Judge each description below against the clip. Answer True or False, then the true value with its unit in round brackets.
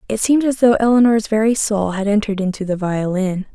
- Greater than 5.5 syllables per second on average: True (6.0 syllables/s)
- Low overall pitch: False (210 Hz)